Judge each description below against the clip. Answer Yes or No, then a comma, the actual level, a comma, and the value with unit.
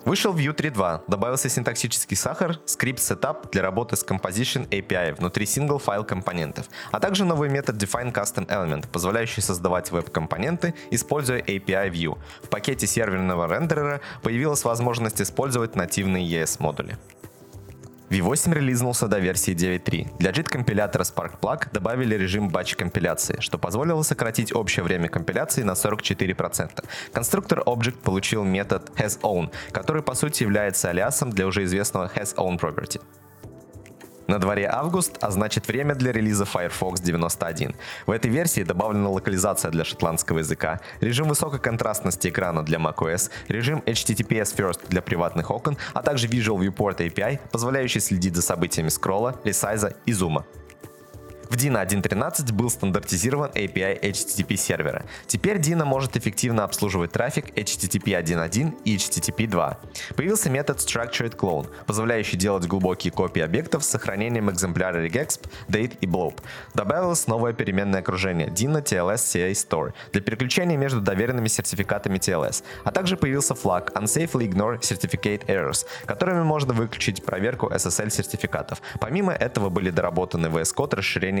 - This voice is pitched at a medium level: No, low, 110 Hz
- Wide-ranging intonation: Yes, wide, 5.7 semitones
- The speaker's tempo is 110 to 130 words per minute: No, average, 140 wpm